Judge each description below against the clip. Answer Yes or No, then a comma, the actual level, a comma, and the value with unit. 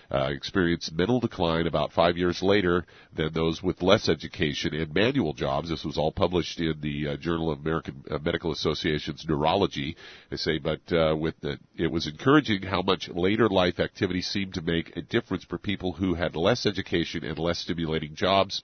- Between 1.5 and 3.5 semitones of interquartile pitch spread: Yes, average, 2.8 semitones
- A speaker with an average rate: Yes, average, 190 wpm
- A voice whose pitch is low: Yes, very low, 85 Hz